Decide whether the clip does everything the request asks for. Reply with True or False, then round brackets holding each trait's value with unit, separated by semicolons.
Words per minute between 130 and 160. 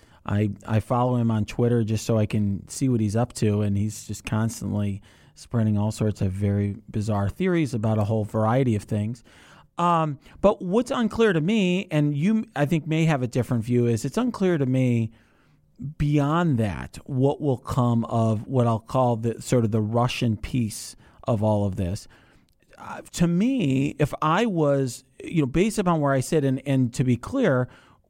False (190 wpm)